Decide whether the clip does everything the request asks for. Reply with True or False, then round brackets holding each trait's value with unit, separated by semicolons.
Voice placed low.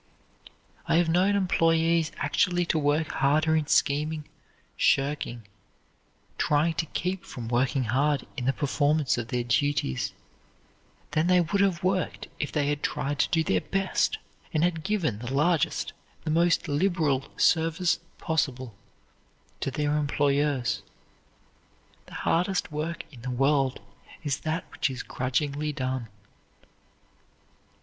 False (150 Hz)